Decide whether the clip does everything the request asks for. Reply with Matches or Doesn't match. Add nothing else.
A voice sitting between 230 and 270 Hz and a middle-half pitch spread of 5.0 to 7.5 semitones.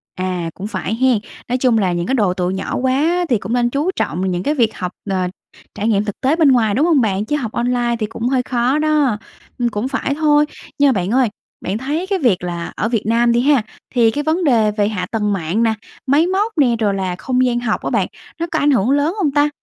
Matches